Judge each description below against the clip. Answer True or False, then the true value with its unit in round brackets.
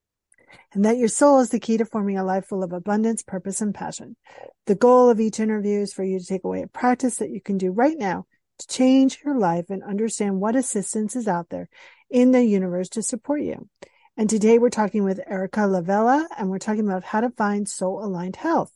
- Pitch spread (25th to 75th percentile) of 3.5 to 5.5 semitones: True (4.0 semitones)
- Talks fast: True (225 wpm)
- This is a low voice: False (215 Hz)